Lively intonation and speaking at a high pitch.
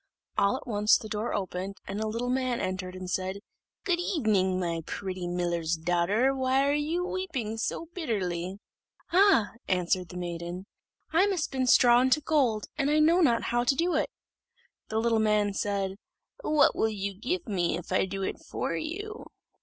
Yes: wide, 6.5 semitones; high, 215 Hz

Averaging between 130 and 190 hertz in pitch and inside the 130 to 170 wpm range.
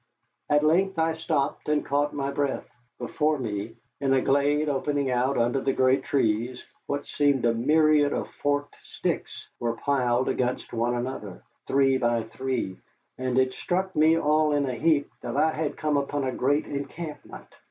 Yes: medium, 140 Hz; average, 165 wpm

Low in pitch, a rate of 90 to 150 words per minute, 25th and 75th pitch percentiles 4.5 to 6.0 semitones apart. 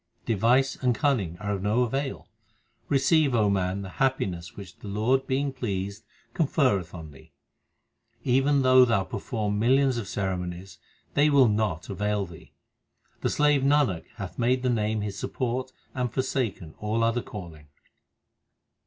Yes: low, 110 Hz; average, 145 wpm; average, 5.1 semitones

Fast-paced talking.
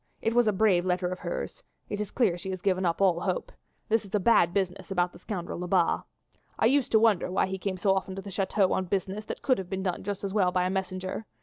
Yes: fast, 265 wpm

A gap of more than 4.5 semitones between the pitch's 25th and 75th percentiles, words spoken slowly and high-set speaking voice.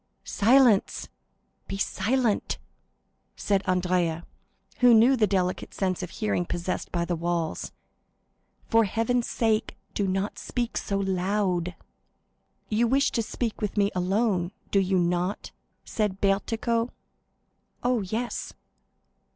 No: average, 3.9 semitones; slow, 115 wpm; high, 200 Hz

